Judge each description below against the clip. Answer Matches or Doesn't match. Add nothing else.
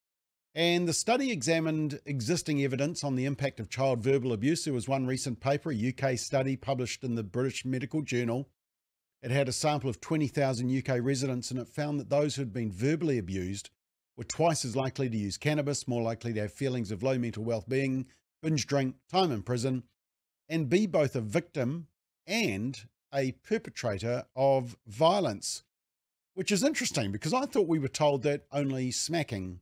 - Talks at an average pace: Matches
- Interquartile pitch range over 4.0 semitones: Doesn't match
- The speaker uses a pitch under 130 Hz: Doesn't match